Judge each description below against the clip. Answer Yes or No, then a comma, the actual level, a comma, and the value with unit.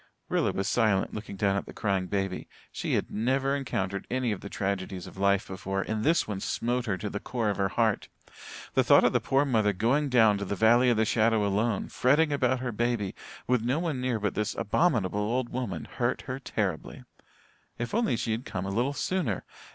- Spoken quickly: Yes, fast, 215 wpm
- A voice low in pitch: Yes, low, 110 Hz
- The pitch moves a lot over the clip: No, average, 4.2 semitones